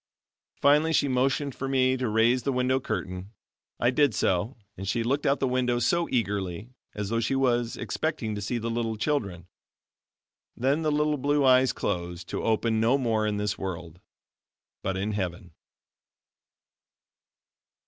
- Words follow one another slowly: No, average, 160 wpm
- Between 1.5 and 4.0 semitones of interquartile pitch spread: No, average, 4.6 semitones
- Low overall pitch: Yes, low, 120 Hz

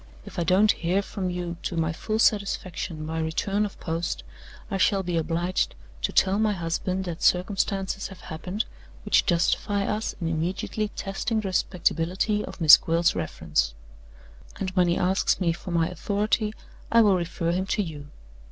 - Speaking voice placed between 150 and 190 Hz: Yes, medium, 185 Hz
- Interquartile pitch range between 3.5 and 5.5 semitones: No, average, 3.0 semitones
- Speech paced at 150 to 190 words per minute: Yes, average, 170 wpm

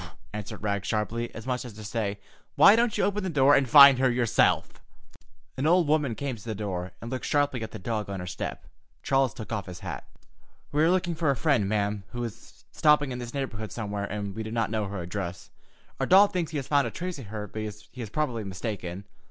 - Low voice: Yes, low, 115 Hz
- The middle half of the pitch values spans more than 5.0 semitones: Yes, wide, 5.4 semitones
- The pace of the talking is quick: Yes, fast, 240 wpm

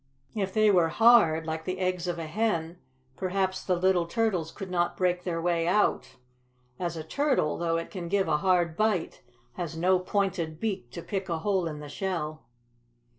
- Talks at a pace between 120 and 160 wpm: No, average, 185 wpm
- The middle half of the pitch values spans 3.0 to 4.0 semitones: No, narrow, 2.6 semitones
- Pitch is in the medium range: Yes, medium, 180 Hz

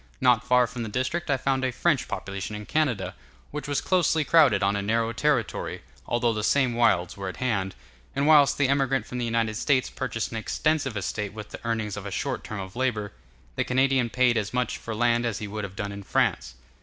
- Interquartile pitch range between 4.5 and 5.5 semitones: No, average, 4.0 semitones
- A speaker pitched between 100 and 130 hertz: Yes, low, 120 Hz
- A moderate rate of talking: No, fast, 220 wpm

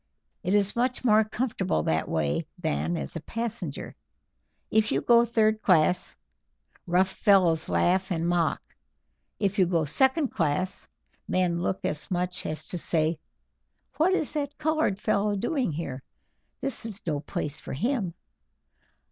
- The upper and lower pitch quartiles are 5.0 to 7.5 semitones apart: Yes, wide, 5.6 semitones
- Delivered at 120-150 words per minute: Yes, average, 145 wpm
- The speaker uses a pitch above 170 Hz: Yes, high, 190 Hz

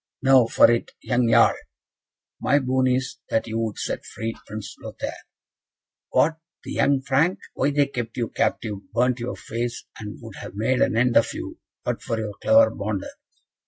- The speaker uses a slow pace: No, average, 175 wpm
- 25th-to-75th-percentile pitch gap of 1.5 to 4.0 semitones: Yes, average, 2.8 semitones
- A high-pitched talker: No, low, 120 Hz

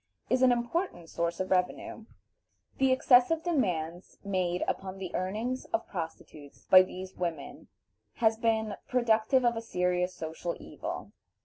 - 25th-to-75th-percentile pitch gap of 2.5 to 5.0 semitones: No, wide, 5.4 semitones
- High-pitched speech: Yes, high, 195 Hz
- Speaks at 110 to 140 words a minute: Yes, slow, 135 wpm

